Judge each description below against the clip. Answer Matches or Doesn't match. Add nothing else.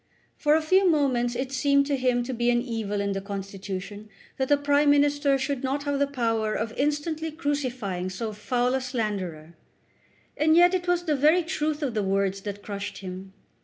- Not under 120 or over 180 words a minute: Doesn't match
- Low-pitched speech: Doesn't match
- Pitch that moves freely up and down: Matches